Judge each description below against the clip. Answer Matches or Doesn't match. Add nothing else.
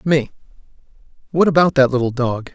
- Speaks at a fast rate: Doesn't match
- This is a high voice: Doesn't match